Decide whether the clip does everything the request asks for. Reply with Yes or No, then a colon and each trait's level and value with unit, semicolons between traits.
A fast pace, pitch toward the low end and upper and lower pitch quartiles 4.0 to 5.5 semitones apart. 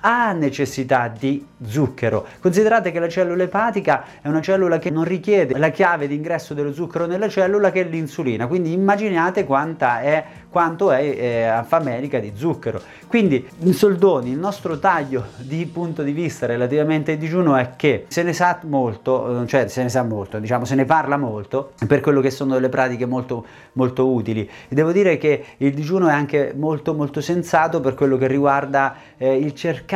No: fast, 185 wpm; medium, 150 Hz; average, 4.7 semitones